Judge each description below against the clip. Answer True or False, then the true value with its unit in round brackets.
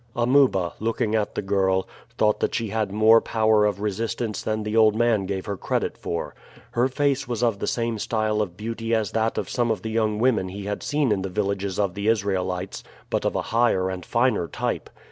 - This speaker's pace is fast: True (215 wpm)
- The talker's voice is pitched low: True (110 Hz)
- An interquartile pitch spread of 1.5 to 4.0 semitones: True (2.5 semitones)